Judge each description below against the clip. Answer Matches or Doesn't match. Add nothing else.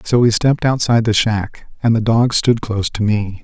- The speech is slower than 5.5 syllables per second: Matches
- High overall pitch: Doesn't match